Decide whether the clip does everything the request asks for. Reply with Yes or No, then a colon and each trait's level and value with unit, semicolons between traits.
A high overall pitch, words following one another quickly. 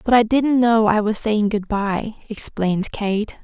No: high, 215 Hz; average, 190 wpm